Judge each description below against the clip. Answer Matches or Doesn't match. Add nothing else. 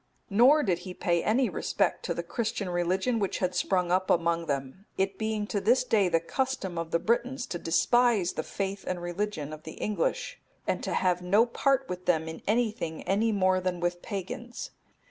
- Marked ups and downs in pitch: Doesn't match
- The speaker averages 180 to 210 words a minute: Matches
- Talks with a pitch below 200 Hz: Matches